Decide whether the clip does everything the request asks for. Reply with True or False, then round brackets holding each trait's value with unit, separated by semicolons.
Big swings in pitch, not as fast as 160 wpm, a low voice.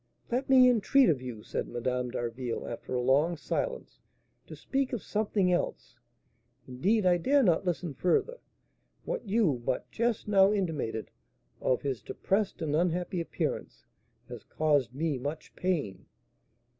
False (8.5 semitones; 145 wpm; 170 Hz)